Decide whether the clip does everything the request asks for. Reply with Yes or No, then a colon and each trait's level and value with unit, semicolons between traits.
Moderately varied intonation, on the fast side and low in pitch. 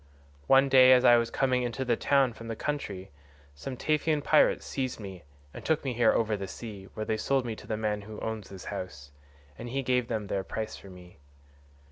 Yes: average, 4.2 semitones; fast, 215 wpm; low, 115 Hz